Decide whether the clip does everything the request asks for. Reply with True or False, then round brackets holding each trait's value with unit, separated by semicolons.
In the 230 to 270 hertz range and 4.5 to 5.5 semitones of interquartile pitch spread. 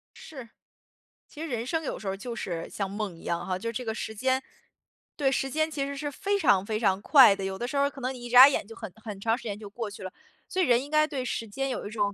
True (235 Hz; 5.1 semitones)